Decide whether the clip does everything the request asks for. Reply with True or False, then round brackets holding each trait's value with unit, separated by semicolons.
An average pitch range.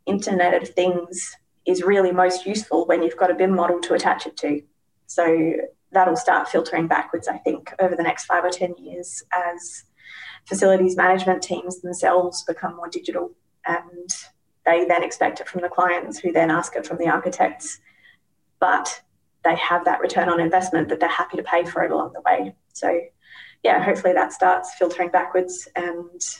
False (1.0 semitones)